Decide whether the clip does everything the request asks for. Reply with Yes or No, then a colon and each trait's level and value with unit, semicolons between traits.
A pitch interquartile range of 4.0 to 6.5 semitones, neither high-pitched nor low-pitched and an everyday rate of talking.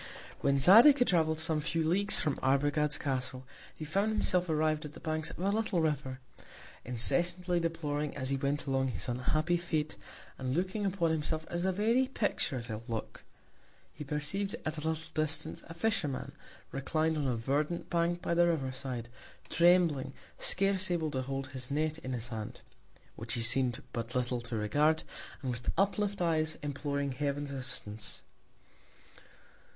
Yes: average, 4.5 semitones; medium, 150 Hz; average, 165 wpm